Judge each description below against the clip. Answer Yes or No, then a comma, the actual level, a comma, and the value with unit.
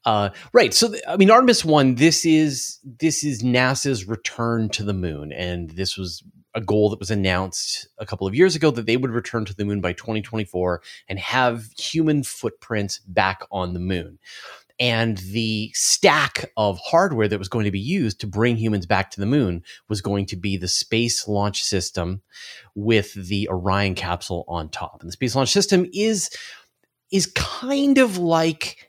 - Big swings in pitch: Yes, wide, 5.8 semitones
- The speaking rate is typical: Yes, average, 185 wpm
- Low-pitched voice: Yes, low, 110 Hz